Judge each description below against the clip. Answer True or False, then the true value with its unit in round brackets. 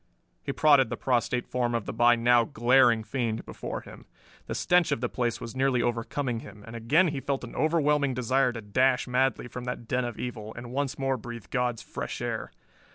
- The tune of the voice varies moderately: False (2.3 semitones)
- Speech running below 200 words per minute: False (205 wpm)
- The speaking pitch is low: True (125 Hz)